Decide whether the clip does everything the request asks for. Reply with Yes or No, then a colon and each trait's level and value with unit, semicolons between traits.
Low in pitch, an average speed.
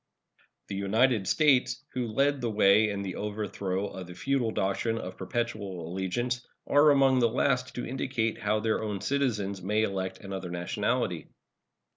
Yes: low, 110 Hz; average, 155 wpm